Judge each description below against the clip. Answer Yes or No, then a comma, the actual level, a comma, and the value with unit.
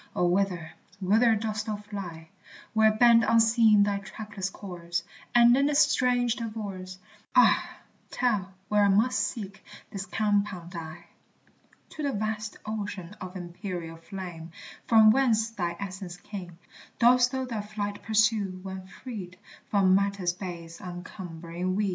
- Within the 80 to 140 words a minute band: Yes, slow, 135 wpm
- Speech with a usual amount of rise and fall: Yes, average, 3.3 semitones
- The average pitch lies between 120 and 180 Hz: No, high, 200 Hz